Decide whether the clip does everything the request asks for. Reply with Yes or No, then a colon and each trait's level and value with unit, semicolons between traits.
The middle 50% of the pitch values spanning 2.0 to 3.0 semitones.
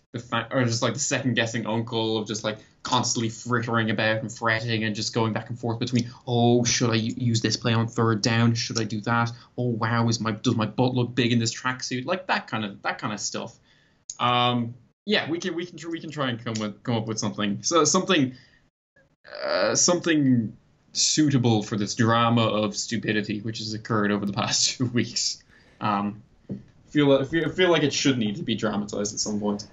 Yes: narrow, 2.4 semitones